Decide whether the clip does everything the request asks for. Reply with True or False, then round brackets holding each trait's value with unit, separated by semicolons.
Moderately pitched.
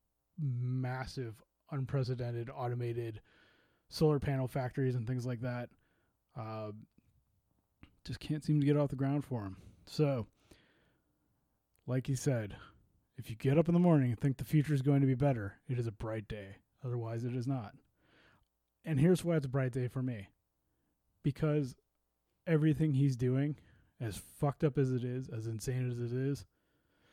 False (130 Hz)